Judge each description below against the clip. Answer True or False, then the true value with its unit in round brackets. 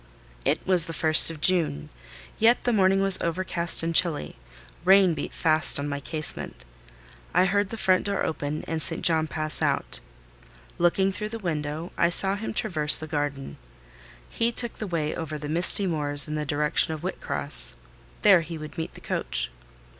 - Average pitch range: True (3.9 semitones)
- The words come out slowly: False (175 wpm)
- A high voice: False (165 Hz)